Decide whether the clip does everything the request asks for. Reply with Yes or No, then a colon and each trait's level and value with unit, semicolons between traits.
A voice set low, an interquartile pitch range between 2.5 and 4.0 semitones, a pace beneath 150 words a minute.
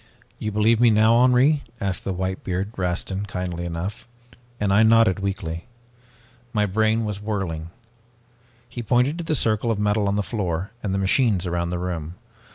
No: low, 100 Hz; average, 3.5 semitones; average, 165 wpm